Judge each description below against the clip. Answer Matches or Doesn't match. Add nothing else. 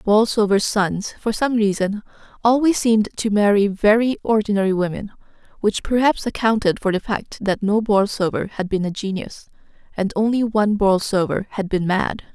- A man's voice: Doesn't match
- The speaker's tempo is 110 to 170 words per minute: Matches